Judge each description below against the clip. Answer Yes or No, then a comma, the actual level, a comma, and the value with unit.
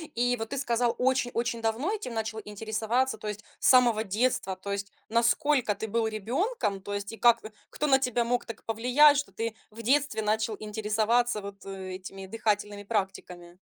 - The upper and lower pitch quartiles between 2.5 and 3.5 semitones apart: Yes, average, 2.8 semitones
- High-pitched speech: Yes, high, 225 Hz